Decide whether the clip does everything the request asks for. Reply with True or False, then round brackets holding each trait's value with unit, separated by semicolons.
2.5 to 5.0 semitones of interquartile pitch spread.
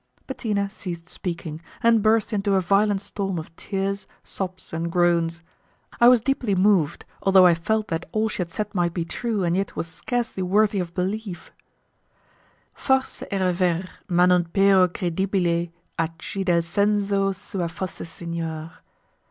True (3.1 semitones)